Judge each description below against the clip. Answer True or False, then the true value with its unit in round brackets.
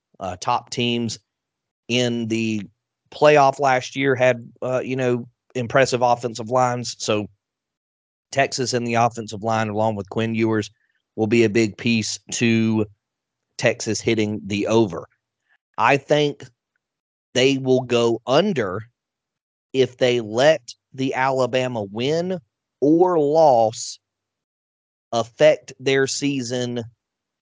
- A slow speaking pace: True (115 wpm)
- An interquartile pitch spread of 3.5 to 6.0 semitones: False (2.8 semitones)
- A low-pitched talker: True (120 Hz)